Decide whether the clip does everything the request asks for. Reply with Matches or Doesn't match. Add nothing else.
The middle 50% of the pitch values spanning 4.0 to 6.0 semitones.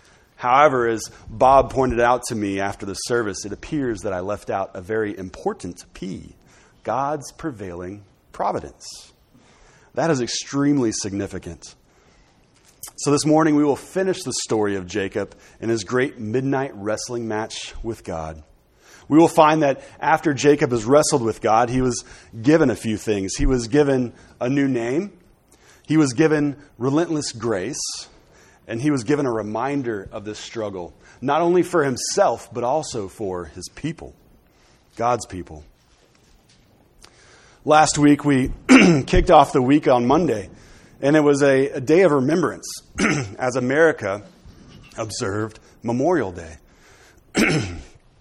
Matches